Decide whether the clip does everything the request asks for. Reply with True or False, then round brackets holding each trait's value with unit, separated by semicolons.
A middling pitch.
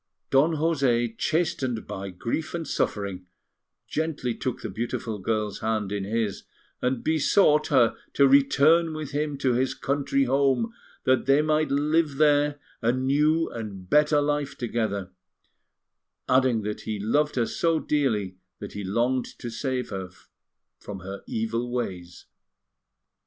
False (130 Hz)